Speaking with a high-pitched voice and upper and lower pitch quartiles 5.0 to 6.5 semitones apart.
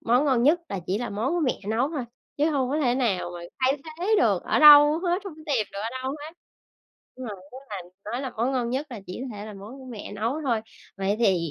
Yes: very high, 255 Hz; wide, 5.4 semitones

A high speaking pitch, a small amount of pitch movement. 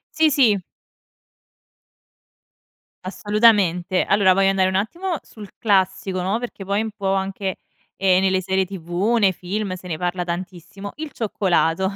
Yes: high, 195 Hz; narrow, 2.1 semitones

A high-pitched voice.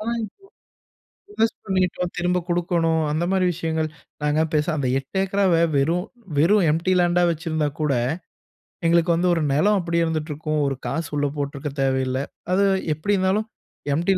No: medium, 165 Hz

